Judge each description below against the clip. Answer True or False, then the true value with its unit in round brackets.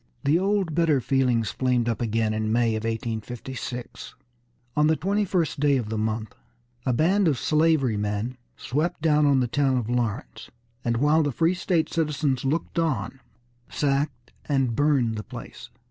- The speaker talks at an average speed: True (160 wpm)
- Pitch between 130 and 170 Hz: True (135 Hz)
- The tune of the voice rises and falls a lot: False (5.0 semitones)